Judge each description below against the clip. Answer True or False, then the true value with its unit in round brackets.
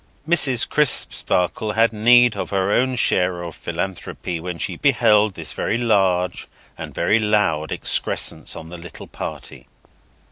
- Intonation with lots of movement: False (4.5 semitones)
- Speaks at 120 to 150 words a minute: True (140 wpm)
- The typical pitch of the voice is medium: False (100 Hz)